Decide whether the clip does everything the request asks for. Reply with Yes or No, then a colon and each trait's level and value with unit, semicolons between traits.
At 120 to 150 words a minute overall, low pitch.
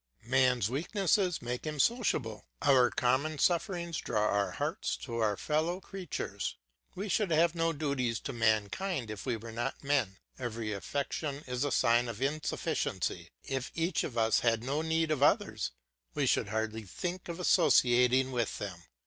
No: average, 160 wpm; low, 130 Hz